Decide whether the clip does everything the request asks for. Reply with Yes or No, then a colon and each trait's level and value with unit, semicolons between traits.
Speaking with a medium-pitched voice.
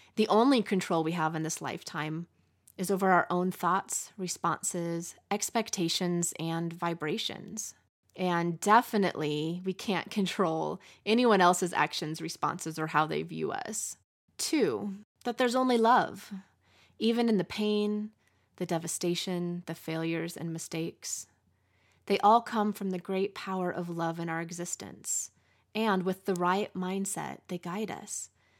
Yes: medium, 180 Hz